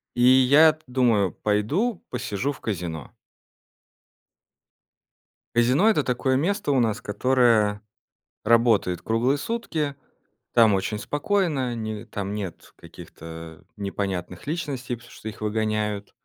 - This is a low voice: Yes, low, 115 Hz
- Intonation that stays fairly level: No, average, 4.9 semitones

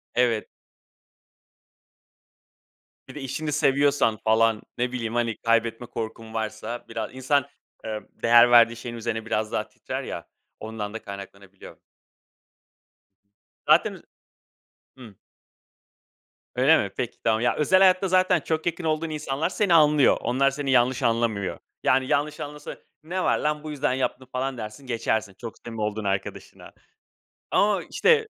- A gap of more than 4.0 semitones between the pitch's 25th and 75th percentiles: Yes, average, 4.9 semitones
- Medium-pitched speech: No, low, 125 Hz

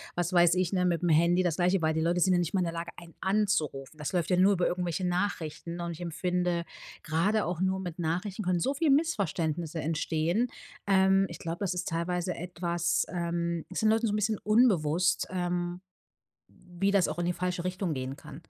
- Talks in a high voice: No, medium, 175 Hz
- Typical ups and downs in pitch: No, narrow, 2.0 semitones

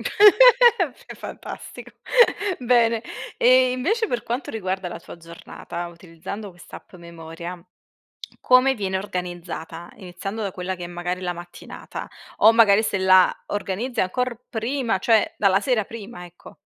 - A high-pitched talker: Yes, high, 200 Hz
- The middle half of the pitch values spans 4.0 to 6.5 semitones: Yes, average, 5.2 semitones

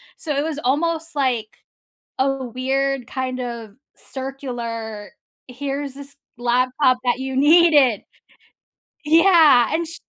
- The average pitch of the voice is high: Yes, very high, 265 Hz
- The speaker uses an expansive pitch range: No, average, 3.0 semitones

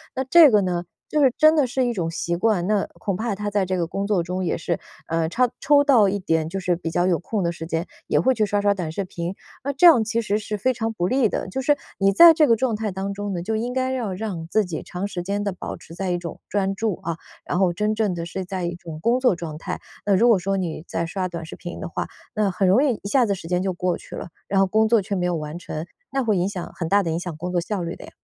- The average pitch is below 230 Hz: Yes, high, 195 Hz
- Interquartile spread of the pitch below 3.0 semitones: No, average, 4.0 semitones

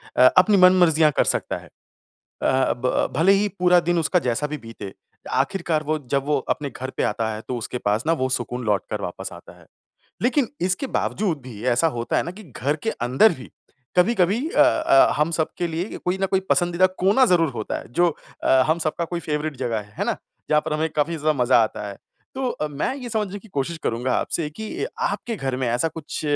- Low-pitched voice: No, medium, 160 Hz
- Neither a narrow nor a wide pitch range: No, wide, 6.2 semitones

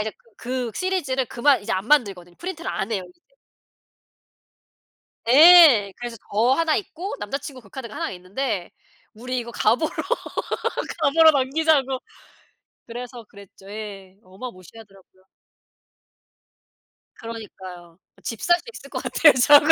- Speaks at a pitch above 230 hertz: Yes, high, 240 Hz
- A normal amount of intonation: No, wide, 6.5 semitones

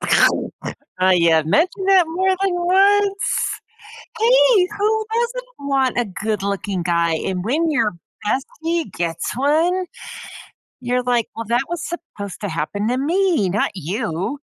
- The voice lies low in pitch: No, very high, 270 Hz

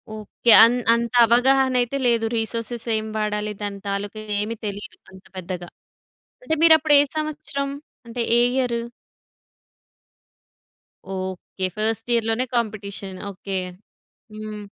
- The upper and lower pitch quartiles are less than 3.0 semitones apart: No, average, 3.3 semitones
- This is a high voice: Yes, high, 225 Hz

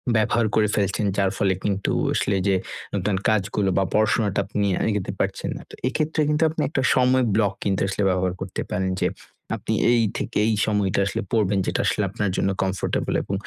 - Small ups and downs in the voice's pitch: Yes, narrow, 2.3 semitones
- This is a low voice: Yes, low, 105 Hz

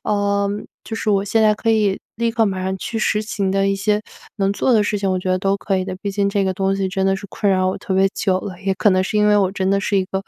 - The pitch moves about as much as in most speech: No, narrow, 1.5 semitones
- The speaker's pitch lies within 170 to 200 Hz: Yes, high, 195 Hz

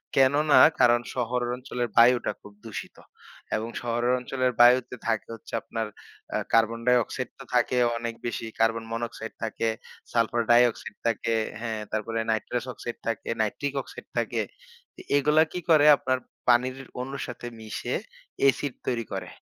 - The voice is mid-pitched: No, low, 120 Hz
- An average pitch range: No, narrow, 1.9 semitones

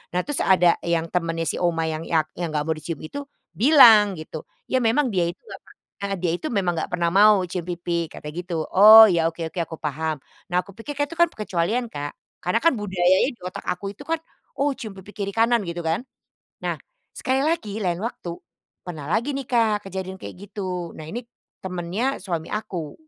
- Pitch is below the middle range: No, medium, 185 Hz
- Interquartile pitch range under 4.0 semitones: No, average, 4.7 semitones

